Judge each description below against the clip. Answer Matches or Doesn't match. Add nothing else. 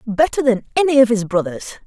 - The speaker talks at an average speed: Matches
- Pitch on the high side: Matches